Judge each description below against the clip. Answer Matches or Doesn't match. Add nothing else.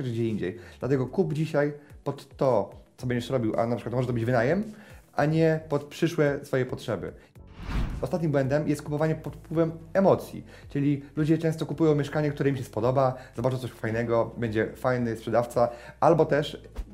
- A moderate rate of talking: Doesn't match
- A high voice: Doesn't match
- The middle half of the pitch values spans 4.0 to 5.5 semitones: Matches